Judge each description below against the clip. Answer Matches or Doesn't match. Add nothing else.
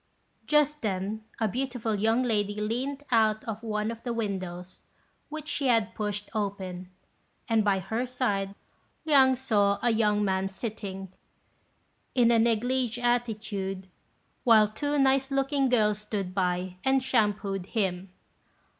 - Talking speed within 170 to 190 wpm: Doesn't match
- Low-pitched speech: Doesn't match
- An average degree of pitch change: Matches